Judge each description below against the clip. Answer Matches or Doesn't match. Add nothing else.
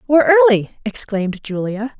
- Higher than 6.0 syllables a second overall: Matches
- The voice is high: Matches